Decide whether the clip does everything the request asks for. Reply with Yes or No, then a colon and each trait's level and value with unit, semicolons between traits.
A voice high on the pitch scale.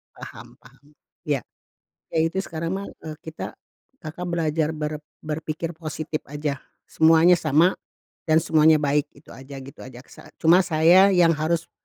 No: medium, 160 Hz